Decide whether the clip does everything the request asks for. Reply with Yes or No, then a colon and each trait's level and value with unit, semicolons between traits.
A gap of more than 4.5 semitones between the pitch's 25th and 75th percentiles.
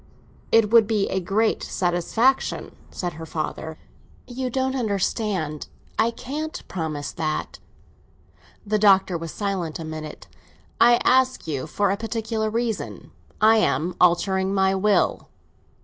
Yes: average, 5.0 semitones